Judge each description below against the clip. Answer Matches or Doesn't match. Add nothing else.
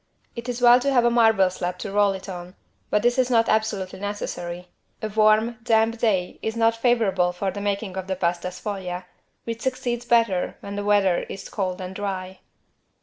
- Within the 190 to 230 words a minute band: Matches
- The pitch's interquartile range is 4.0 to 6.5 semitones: Doesn't match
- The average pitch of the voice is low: Doesn't match